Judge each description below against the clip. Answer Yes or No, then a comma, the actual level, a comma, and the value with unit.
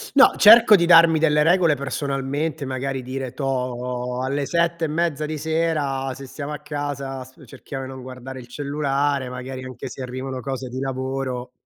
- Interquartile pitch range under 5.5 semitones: Yes, narrow, 2.6 semitones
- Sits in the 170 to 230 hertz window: No, low, 135 Hz